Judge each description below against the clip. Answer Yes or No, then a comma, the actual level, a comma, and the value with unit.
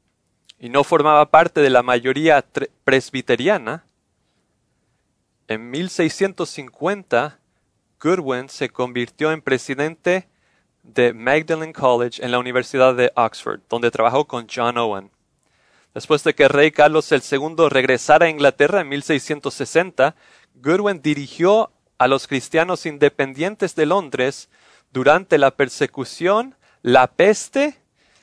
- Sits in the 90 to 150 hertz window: Yes, medium, 140 Hz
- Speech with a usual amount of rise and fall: Yes, average, 4.3 semitones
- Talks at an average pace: No, slow, 110 wpm